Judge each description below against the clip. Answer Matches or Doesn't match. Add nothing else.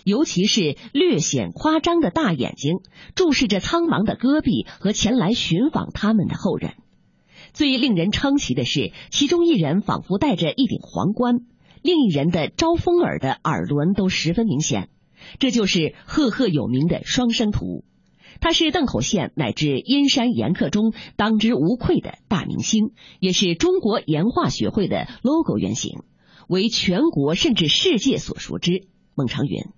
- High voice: Matches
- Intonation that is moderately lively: Doesn't match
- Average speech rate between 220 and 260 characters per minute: Matches